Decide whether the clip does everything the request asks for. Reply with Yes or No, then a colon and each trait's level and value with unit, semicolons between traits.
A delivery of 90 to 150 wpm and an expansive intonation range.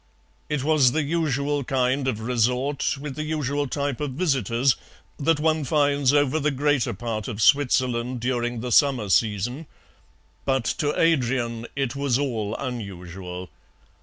No: average, 140 wpm; average, 3.4 semitones